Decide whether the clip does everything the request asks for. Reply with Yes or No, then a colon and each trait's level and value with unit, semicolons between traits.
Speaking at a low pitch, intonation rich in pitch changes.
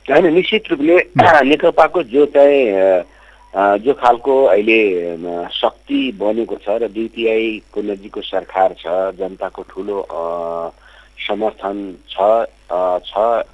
Yes: low, 105 Hz; wide, 6.8 semitones